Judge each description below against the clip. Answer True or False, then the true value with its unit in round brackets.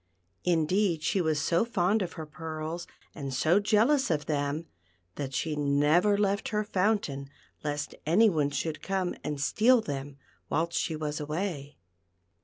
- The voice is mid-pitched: True (160 Hz)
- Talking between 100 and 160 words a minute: True (145 wpm)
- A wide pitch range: False (4.9 semitones)